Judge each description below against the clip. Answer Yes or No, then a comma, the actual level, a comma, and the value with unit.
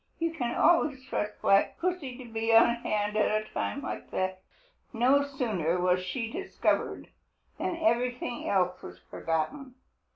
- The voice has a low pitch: No, high, 235 Hz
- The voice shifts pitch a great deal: Yes, wide, 5.7 semitones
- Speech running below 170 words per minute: Yes, average, 150 wpm